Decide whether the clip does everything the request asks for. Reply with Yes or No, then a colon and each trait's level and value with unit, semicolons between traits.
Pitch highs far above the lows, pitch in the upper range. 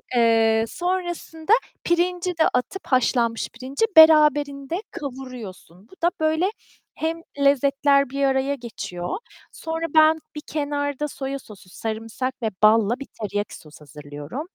Yes: wide, 5.7 semitones; very high, 275 Hz